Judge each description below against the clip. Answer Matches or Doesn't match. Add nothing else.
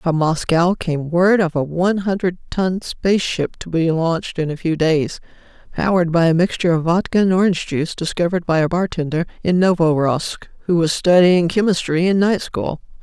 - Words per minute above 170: Matches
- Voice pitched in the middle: Matches